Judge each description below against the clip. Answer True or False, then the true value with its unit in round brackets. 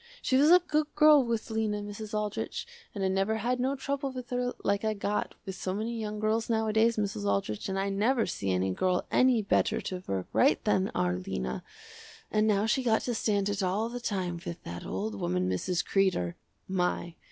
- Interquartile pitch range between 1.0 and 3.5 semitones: False (4.2 semitones)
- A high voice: True (210 Hz)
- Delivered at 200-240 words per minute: True (205 wpm)